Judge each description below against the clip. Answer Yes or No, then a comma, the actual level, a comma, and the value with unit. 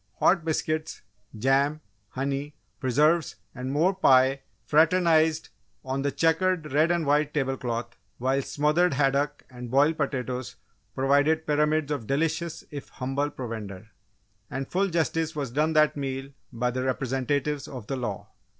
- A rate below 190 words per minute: Yes, average, 140 wpm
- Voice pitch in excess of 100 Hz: Yes, medium, 140 Hz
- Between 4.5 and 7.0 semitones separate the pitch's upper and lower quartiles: No, average, 3.1 semitones